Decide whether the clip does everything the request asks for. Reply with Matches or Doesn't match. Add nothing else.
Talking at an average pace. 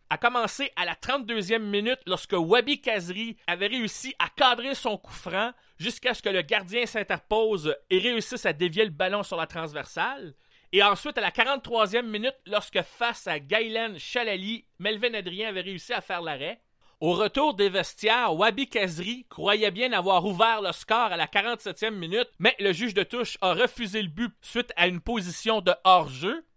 Matches